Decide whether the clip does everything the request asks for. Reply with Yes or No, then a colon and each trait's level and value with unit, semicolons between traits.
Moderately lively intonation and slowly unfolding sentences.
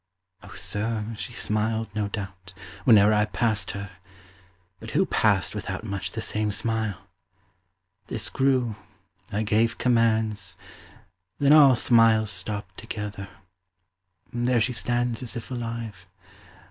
No: narrow, 2.3 semitones; slow, 120 wpm